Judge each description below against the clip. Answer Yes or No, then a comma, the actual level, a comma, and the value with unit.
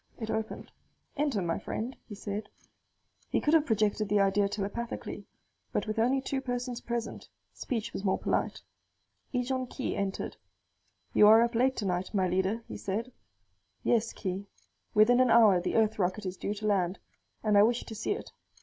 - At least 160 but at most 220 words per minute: Yes, average, 175 wpm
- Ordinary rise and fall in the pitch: Yes, average, 3.3 semitones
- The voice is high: Yes, high, 215 Hz